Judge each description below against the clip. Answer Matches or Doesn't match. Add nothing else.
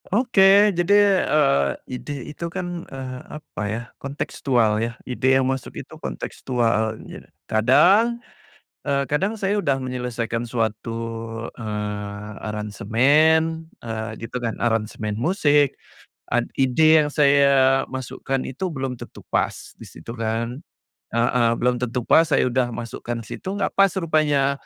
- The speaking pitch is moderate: Doesn't match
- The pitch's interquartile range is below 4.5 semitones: Doesn't match